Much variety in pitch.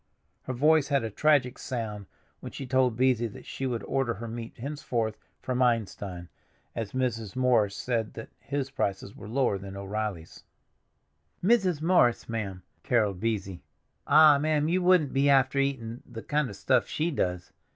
No: average, 4.4 semitones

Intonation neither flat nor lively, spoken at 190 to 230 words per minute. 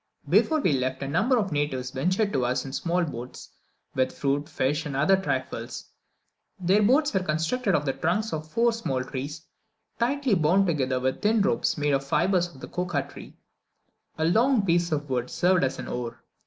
No: wide, 6.3 semitones; average, 195 wpm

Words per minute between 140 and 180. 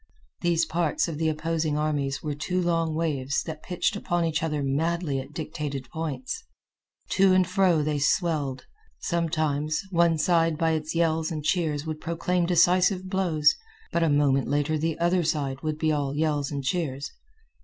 Yes: average, 165 wpm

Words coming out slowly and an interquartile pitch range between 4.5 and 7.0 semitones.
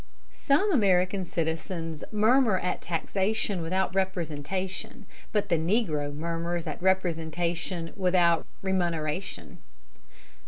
No: slow, 90 wpm; average, 2.7 semitones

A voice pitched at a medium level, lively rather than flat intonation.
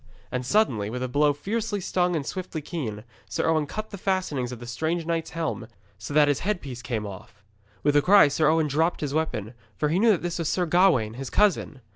Yes: medium, 155 Hz; wide, 5.7 semitones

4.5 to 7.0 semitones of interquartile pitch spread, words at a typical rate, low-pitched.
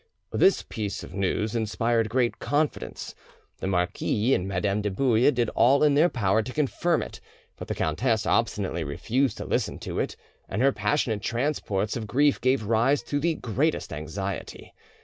Yes: average, 5.2 semitones; average, 170 wpm; low, 115 Hz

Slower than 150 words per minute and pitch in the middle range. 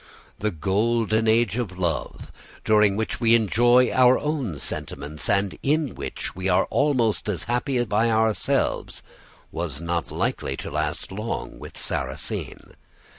No: slow, 135 wpm; low, 110 Hz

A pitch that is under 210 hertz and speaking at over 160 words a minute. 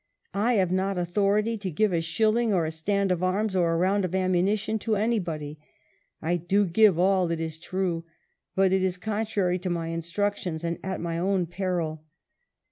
Yes: medium, 185 Hz; average, 185 wpm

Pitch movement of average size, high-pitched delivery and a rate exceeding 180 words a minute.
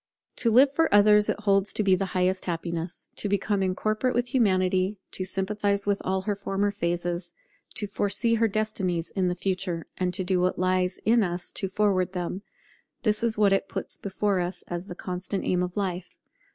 No: narrow, 2.3 semitones; high, 195 Hz; average, 190 wpm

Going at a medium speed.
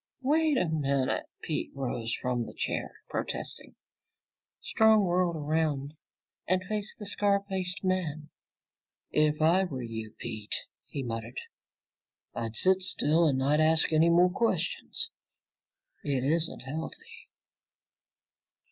No: slow, 120 wpm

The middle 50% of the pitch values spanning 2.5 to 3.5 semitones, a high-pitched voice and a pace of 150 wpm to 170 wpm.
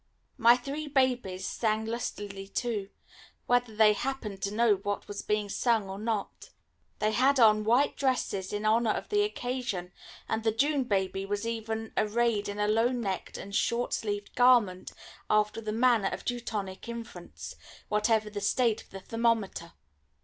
Yes: average, 2.8 semitones; high, 220 Hz; average, 160 wpm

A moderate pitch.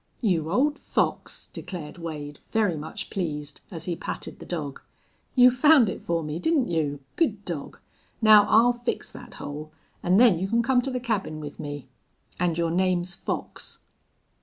Yes: medium, 180 Hz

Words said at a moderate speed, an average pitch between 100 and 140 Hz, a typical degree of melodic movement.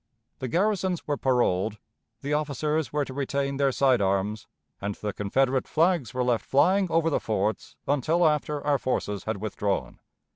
No: average, 160 wpm; low, 135 Hz; wide, 5.8 semitones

